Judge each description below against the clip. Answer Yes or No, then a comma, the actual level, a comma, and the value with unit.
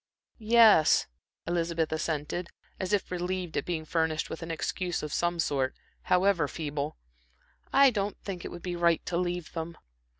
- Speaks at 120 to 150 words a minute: No, average, 160 wpm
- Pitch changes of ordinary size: No, narrow, 2.2 semitones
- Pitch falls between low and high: Yes, medium, 170 Hz